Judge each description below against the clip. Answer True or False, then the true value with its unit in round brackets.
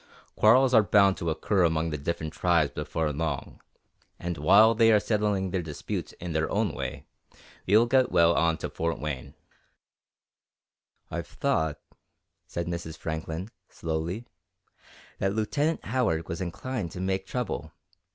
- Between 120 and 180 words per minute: True (140 wpm)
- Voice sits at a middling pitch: False (85 Hz)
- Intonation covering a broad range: False (4.8 semitones)